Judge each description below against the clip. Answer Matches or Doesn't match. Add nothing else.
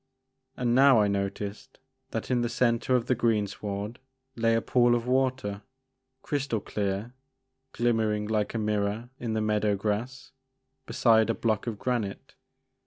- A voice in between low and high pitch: Doesn't match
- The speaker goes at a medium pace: Matches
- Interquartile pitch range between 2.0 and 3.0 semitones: Matches